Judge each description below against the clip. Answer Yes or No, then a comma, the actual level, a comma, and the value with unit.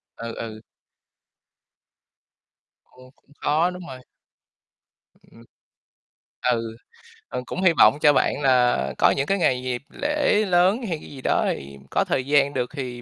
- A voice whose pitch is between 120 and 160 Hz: Yes, low, 135 Hz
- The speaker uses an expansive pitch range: Yes, wide, 6.2 semitones